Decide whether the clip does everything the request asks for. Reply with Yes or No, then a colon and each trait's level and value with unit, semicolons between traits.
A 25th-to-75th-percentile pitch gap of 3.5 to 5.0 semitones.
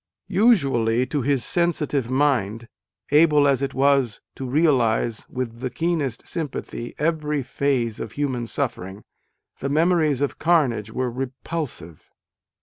Yes: average, 4.0 semitones